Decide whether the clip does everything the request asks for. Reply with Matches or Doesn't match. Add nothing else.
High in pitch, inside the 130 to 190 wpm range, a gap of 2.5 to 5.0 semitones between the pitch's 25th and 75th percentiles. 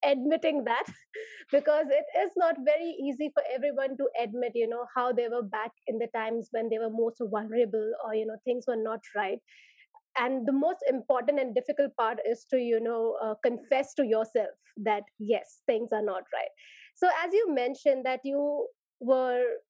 Matches